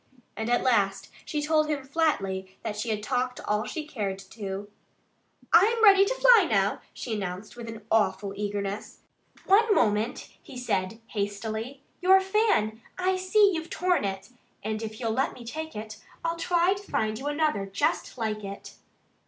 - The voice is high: Yes, high, 230 Hz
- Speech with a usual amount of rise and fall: No, wide, 7.6 semitones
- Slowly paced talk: No, average, 170 wpm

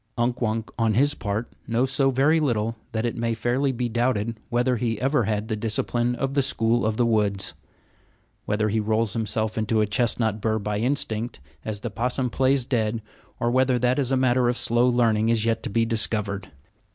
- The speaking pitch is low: Yes, low, 115 Hz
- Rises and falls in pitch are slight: Yes, narrow, 2.3 semitones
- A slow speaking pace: No, average, 200 wpm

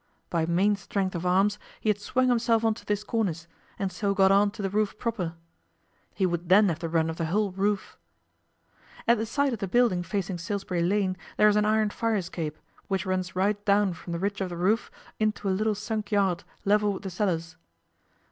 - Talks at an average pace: No, fast, 215 wpm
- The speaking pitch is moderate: No, high, 200 Hz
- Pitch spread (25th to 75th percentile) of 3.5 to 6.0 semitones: No, average, 2.8 semitones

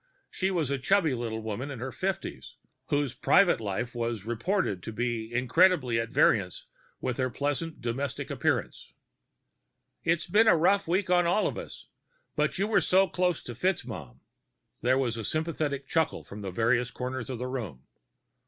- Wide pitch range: Yes, wide, 6.7 semitones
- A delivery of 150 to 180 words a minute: Yes, average, 160 wpm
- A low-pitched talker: Yes, low, 130 Hz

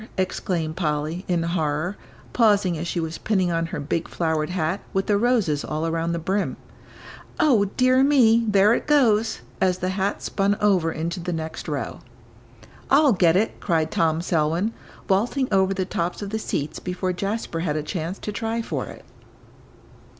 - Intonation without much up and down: No, average, 4.1 semitones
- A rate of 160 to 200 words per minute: Yes, average, 170 wpm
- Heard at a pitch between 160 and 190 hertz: Yes, medium, 185 Hz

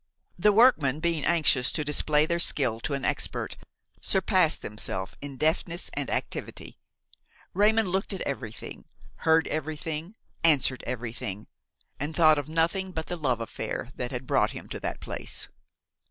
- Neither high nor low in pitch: Yes, medium, 155 Hz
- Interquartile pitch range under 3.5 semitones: No, average, 4.6 semitones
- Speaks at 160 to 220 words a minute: No, average, 145 wpm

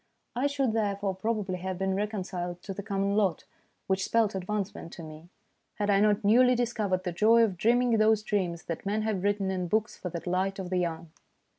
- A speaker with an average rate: No, fast, 210 wpm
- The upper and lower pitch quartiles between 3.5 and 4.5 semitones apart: No, average, 2.8 semitones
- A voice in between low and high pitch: No, high, 200 Hz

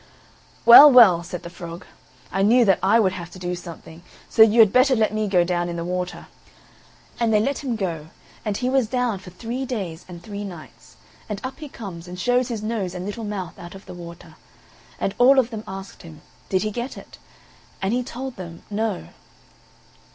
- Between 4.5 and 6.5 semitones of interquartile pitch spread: Yes, average, 4.9 semitones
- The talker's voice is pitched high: Yes, high, 200 Hz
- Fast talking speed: Yes, fast, 210 wpm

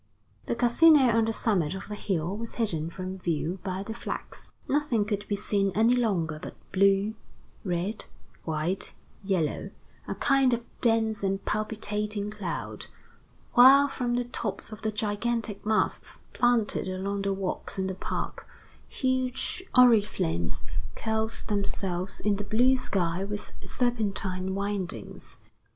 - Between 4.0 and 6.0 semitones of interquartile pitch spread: No, average, 3.4 semitones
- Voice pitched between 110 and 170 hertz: No, high, 205 Hz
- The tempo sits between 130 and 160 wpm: Yes, slow, 135 wpm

